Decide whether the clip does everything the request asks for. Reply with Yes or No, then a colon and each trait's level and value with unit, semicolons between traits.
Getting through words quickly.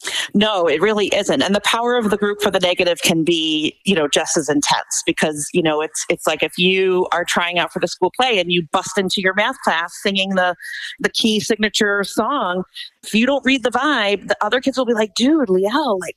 Yes: fast, 235 wpm